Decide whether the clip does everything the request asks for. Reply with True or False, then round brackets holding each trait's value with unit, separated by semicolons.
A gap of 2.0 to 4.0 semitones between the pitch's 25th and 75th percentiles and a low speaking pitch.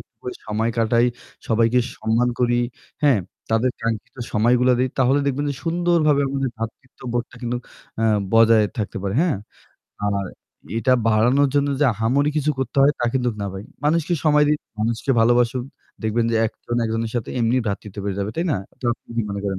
True (3.6 semitones; 120 Hz)